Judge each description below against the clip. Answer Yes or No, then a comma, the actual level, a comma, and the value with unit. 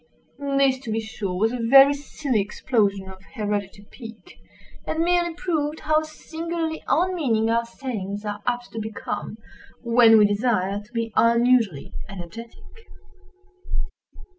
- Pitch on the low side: No, high, 235 Hz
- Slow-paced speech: Yes, slow, 130 wpm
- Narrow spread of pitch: No, average, 5.2 semitones